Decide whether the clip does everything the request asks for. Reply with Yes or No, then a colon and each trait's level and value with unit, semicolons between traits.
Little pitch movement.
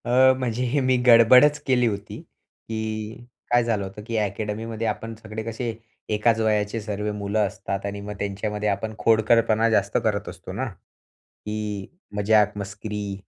Yes: narrow, 1.8 semitones